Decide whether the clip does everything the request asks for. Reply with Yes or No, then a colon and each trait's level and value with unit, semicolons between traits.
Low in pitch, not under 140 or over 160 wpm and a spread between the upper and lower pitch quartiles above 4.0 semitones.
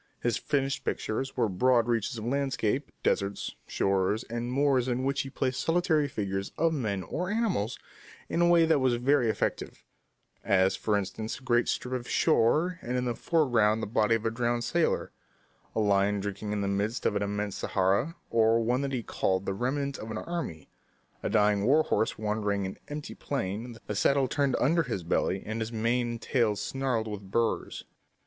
No: low, 115 Hz; average, 190 wpm; average, 4.6 semitones